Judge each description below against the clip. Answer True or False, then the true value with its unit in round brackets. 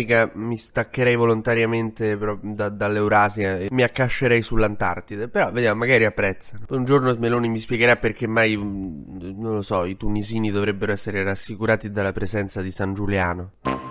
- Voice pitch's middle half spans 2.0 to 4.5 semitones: True (2.5 semitones)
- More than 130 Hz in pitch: False (105 Hz)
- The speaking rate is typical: True (140 wpm)